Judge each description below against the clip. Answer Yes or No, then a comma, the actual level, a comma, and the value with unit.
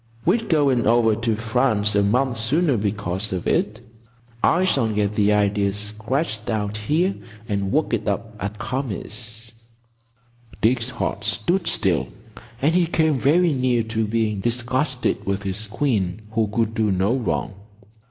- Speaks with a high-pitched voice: No, low, 110 Hz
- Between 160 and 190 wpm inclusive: No, average, 150 wpm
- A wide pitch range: No, average, 3.9 semitones